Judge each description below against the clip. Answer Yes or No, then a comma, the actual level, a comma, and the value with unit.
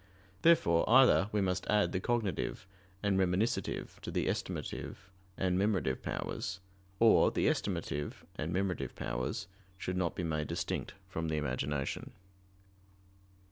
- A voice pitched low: Yes, very low, 90 Hz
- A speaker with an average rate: No, slow, 130 wpm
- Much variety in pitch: No, average, 4.7 semitones